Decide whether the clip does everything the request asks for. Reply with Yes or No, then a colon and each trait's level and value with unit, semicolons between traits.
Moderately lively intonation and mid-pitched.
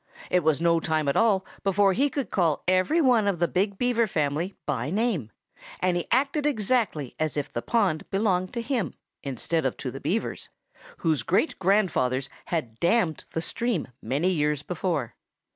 No: wide, 6.2 semitones; medium, 180 Hz